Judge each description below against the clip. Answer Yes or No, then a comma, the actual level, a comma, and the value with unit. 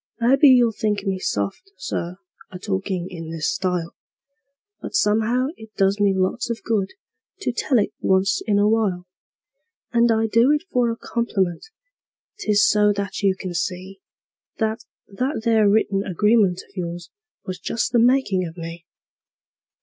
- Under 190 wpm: Yes, average, 155 wpm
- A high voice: Yes, high, 205 Hz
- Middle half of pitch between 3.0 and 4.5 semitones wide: Yes, average, 3.7 semitones